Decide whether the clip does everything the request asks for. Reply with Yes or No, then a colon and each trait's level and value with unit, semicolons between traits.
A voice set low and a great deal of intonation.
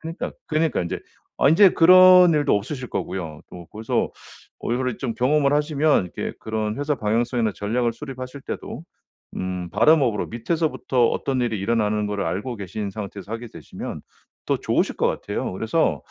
Yes: low, 120 Hz; wide, 6.0 semitones